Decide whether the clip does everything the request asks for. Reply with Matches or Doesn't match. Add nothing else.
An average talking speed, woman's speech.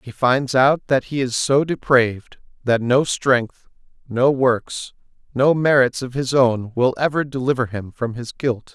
Doesn't match